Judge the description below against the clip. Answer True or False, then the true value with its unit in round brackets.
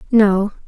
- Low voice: False (205 Hz)